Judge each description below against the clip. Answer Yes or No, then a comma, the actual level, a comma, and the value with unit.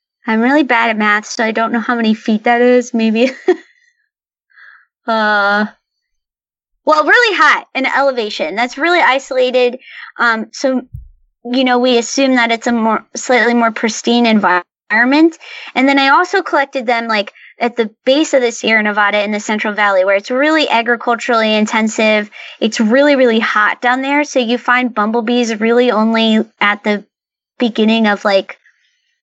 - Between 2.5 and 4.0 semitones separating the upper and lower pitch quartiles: Yes, average, 3.5 semitones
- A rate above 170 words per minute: No, average, 160 wpm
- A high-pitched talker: Yes, high, 240 Hz